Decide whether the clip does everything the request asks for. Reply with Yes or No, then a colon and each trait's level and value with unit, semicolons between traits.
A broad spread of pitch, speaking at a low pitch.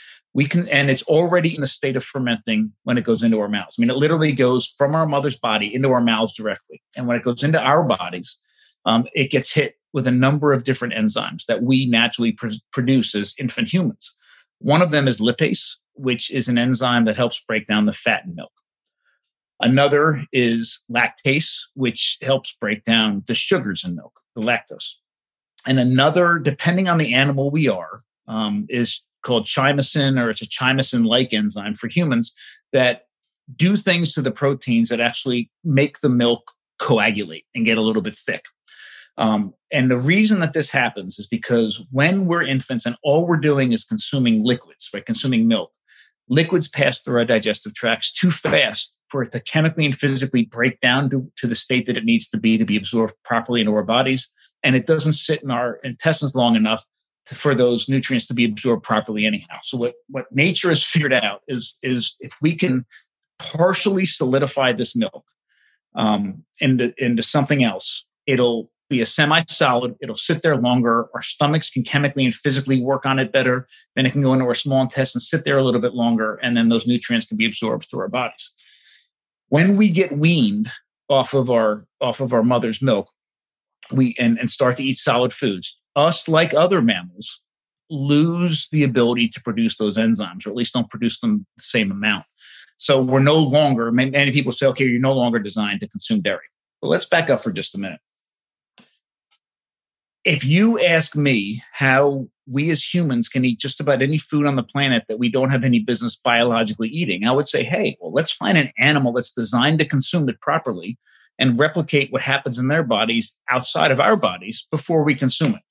No: average, 3.9 semitones; low, 130 Hz